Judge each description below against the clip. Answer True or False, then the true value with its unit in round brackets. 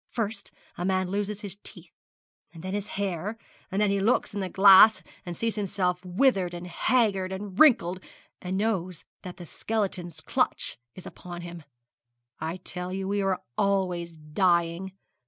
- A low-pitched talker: False (190 Hz)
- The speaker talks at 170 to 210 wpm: False (160 wpm)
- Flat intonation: True (2.3 semitones)